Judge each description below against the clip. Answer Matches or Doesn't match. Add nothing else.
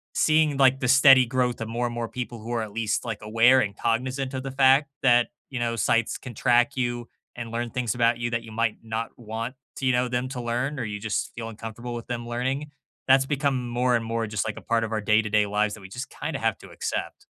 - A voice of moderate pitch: Doesn't match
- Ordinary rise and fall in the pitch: Doesn't match